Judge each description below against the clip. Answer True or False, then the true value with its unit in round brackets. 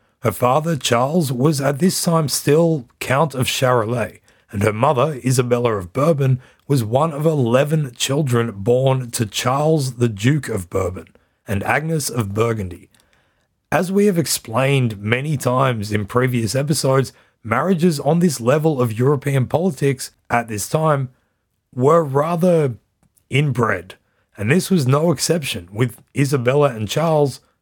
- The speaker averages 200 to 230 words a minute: False (140 wpm)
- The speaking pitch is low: True (130 Hz)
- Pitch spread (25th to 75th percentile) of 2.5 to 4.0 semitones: False (4.4 semitones)